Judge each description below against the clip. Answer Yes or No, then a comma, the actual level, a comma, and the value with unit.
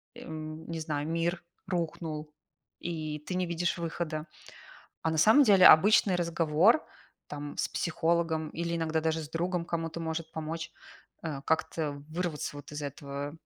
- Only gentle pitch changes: Yes, narrow, 1.7 semitones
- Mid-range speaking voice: Yes, medium, 160 Hz